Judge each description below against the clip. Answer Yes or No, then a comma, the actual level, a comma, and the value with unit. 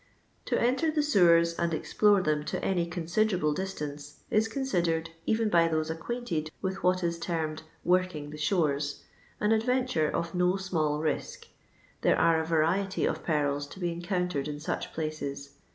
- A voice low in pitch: No, medium, 170 Hz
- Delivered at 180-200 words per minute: No, average, 165 wpm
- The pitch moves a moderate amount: Yes, average, 3.7 semitones